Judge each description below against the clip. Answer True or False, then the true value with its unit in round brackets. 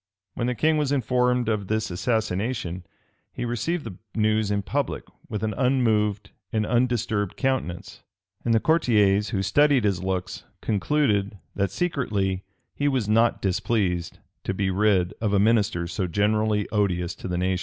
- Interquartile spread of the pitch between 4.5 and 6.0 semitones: False (3.9 semitones)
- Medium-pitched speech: False (105 Hz)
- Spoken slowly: False (160 wpm)